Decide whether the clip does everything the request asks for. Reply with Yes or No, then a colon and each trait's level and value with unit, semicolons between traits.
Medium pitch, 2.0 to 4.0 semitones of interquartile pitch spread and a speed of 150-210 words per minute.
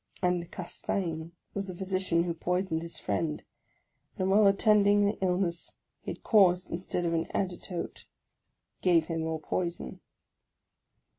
No: medium, 180 Hz; narrow, 2.4 semitones; slow, 135 wpm